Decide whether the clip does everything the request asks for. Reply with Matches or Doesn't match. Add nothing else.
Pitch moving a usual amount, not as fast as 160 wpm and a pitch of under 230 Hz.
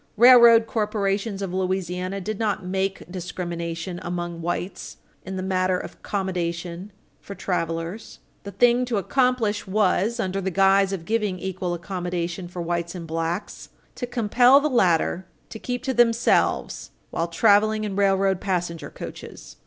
Matches